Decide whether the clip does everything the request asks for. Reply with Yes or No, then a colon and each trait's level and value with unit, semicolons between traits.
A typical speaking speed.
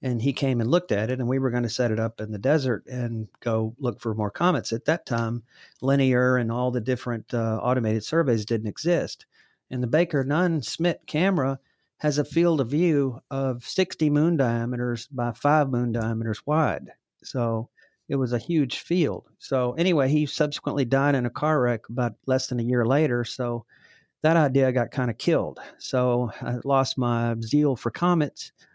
Yes: average, 190 wpm